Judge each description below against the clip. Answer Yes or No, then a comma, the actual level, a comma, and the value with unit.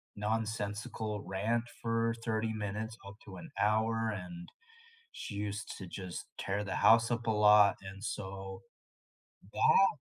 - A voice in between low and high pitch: No, low, 105 Hz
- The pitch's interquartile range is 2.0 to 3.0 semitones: Yes, narrow, 2.4 semitones